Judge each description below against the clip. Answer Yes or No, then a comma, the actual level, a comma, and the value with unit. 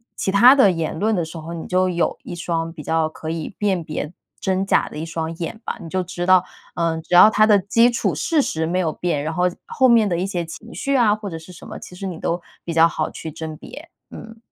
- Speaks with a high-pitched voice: No, medium, 175 Hz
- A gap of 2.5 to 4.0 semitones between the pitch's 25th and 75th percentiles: Yes, average, 3.6 semitones